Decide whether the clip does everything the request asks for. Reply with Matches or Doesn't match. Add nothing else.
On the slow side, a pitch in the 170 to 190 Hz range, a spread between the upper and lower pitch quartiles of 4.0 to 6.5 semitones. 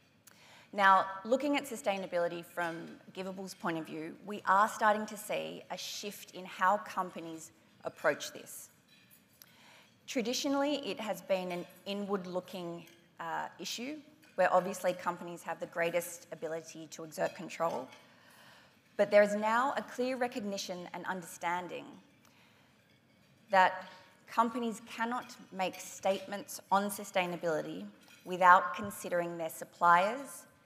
Doesn't match